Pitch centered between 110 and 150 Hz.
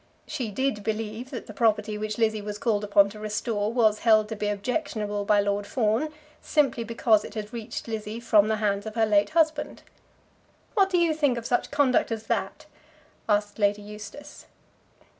No: high, 215 Hz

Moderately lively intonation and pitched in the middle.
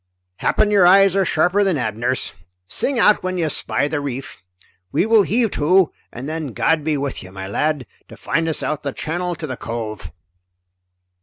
No: wide, 6.0 semitones; medium, 155 Hz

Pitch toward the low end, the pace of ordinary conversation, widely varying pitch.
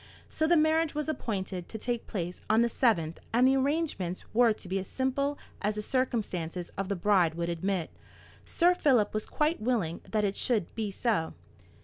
No: high, 215 Hz; average, 190 wpm; wide, 6.0 semitones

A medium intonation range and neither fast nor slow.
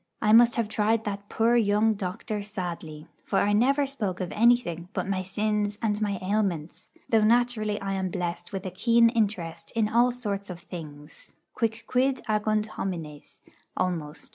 Yes: average, 3.5 semitones; average, 165 wpm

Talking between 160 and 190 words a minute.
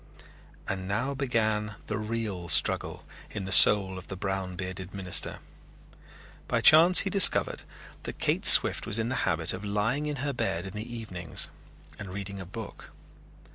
Yes: average, 165 wpm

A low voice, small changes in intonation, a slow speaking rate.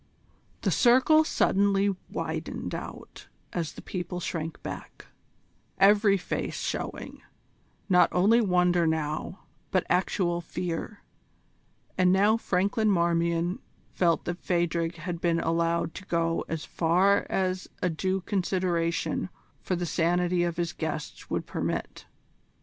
No: medium, 180 Hz; narrow, 2.3 semitones; slow, 120 wpm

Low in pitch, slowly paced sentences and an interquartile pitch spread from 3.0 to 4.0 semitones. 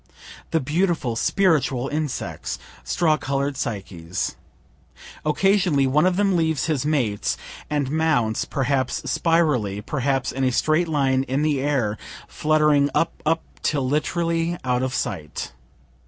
No: medium, 145 Hz; slow, 125 wpm; average, 3.7 semitones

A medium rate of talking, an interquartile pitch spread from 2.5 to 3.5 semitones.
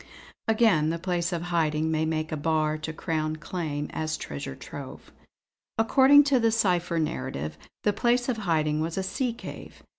No: average, 170 wpm; wide, 5.5 semitones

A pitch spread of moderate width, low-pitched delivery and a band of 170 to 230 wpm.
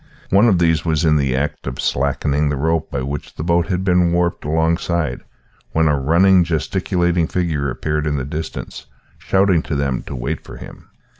Yes: average, 3.1 semitones; very low, 80 Hz; average, 190 wpm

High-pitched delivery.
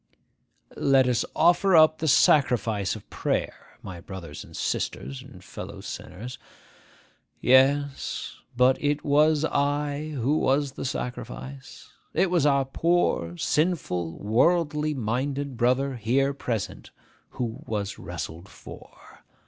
No: low, 135 Hz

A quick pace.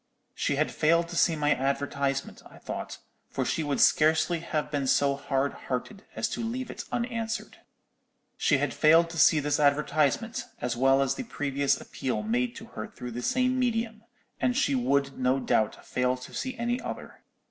No: average, 180 wpm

